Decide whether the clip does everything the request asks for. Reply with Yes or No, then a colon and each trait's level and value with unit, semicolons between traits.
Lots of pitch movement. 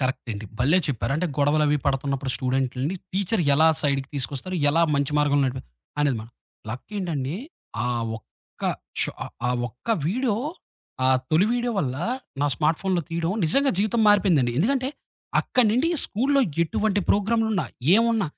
Yes: wide, 7.2 semitones